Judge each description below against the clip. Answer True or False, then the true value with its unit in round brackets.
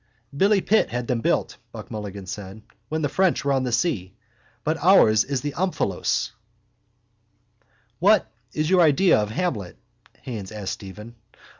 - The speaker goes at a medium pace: True (150 wpm)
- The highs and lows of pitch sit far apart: True (8.4 semitones)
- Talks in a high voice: False (130 Hz)